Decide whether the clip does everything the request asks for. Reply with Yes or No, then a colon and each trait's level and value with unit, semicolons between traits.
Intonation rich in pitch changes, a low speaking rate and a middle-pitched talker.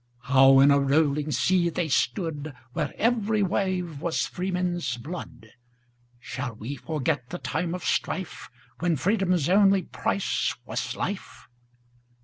Yes: wide, 5.8 semitones; slow, 115 wpm; medium, 155 Hz